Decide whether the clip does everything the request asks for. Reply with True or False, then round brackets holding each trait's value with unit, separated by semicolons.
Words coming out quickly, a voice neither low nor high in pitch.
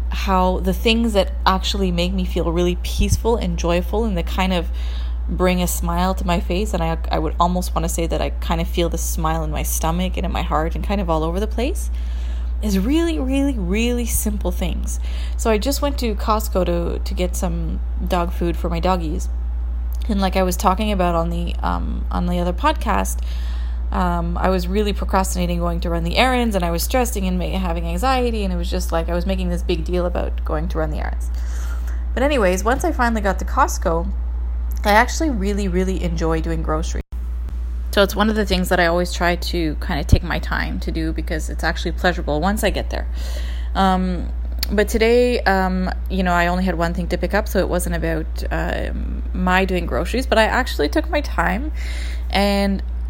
True (215 wpm; 175 Hz)